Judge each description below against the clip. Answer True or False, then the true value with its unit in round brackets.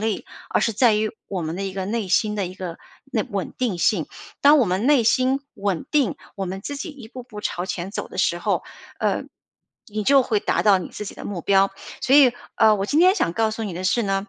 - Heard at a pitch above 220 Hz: False (210 Hz)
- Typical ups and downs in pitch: True (4.2 semitones)